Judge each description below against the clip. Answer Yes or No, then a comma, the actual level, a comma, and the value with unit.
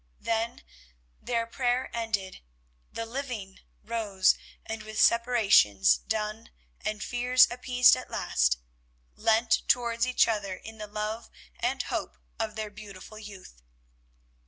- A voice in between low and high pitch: No, high, 220 Hz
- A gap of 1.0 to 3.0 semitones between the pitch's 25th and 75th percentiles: Yes, narrow, 2.5 semitones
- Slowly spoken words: Yes, slow, 120 wpm